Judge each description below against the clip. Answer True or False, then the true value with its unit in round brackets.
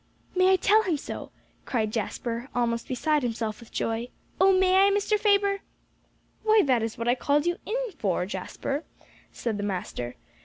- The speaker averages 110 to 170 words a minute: False (180 wpm)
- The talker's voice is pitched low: False (265 Hz)